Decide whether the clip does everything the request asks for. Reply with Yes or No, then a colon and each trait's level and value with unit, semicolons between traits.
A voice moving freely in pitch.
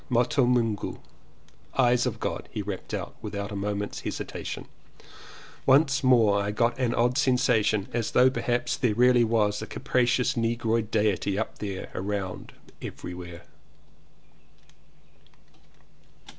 No: average, 3.2 semitones